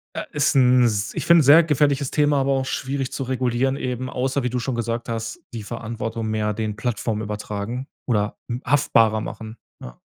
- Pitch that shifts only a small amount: No, average, 3.3 semitones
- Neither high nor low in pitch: No, low, 120 Hz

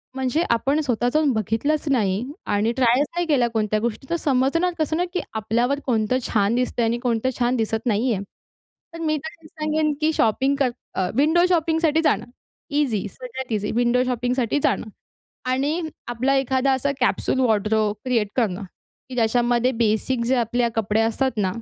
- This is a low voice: No, very high, 250 Hz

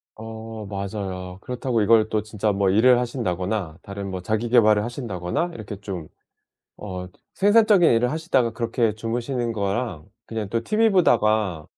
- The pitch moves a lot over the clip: No, average, 3.5 semitones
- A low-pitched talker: Yes, low, 110 Hz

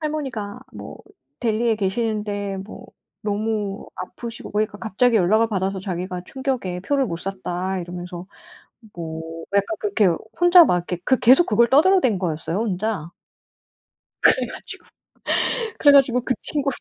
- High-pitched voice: Yes, high, 210 Hz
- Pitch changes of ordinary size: Yes, average, 5.0 semitones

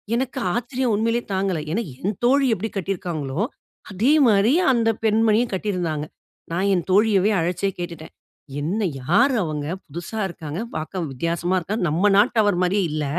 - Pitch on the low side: No, high, 195 Hz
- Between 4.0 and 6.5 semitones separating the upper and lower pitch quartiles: Yes, average, 4.7 semitones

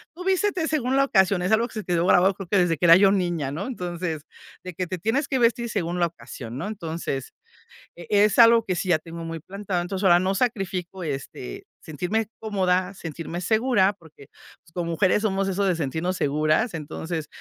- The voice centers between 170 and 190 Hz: Yes, medium, 185 Hz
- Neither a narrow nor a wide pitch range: Yes, average, 3.9 semitones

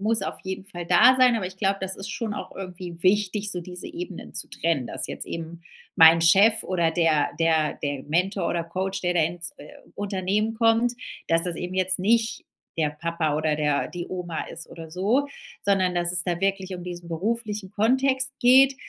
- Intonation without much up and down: No, average, 3.8 semitones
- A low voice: No, medium, 185 Hz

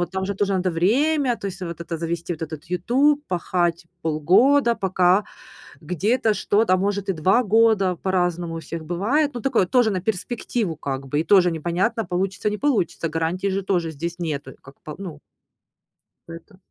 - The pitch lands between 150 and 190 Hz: Yes, medium, 185 Hz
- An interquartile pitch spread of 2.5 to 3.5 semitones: No, average, 3.9 semitones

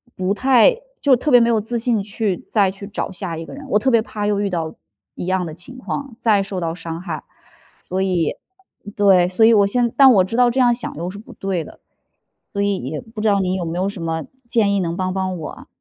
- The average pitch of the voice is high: Yes, high, 200 Hz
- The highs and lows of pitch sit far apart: No, average, 4.0 semitones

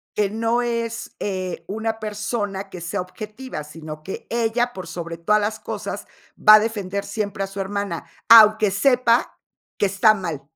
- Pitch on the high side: Yes, high, 205 Hz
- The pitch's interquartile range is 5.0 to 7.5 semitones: No, average, 3.0 semitones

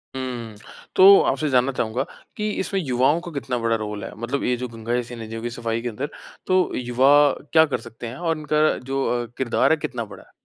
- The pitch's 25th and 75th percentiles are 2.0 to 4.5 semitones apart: Yes, average, 4.0 semitones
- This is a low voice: Yes, low, 125 Hz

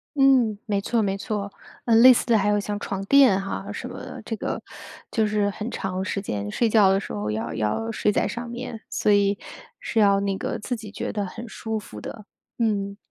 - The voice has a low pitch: No, high, 210 Hz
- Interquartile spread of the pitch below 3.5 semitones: Yes, narrow, 2.4 semitones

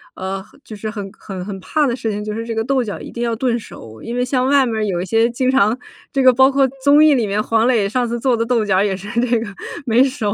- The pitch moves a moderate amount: Yes, average, 3.5 semitones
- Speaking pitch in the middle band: No, high, 230 Hz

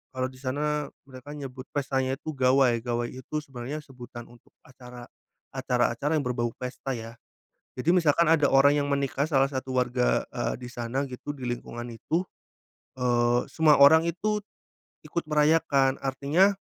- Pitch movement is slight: No, average, 3.0 semitones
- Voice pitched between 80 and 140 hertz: Yes, low, 135 Hz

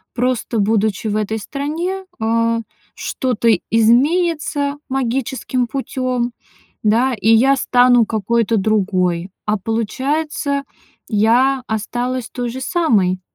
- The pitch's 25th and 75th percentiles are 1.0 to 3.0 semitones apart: No, average, 3.6 semitones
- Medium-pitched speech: No, high, 240 Hz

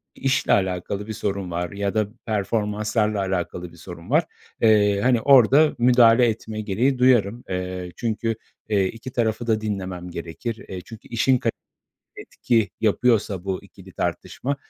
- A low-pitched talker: Yes, low, 105 Hz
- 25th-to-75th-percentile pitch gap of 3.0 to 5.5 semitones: Yes, average, 3.6 semitones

